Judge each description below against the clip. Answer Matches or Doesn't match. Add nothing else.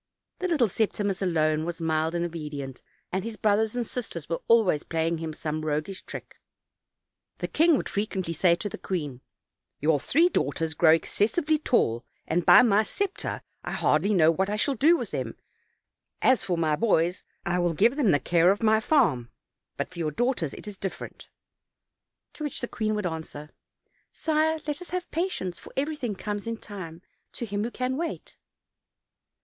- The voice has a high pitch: Matches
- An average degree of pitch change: Doesn't match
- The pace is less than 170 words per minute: Doesn't match